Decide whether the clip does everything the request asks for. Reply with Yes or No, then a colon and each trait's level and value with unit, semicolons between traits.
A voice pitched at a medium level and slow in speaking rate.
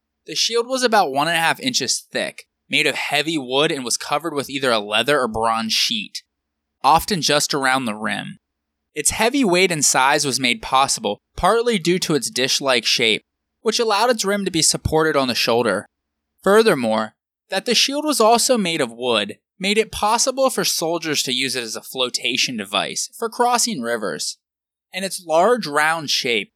No: medium, 160 Hz; average, 180 wpm